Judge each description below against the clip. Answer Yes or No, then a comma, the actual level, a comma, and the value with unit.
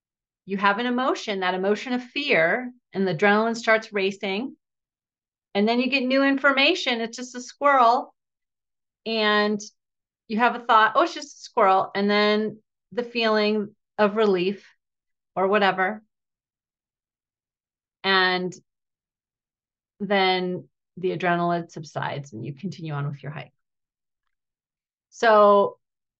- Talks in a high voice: Yes, high, 205 Hz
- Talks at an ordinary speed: No, slow, 125 wpm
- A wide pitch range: No, average, 4.3 semitones